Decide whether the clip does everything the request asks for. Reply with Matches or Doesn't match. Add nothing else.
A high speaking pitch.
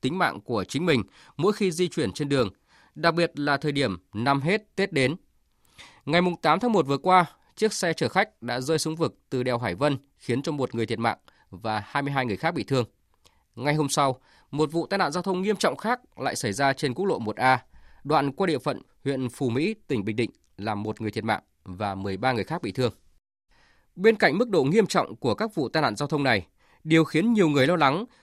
Doesn't match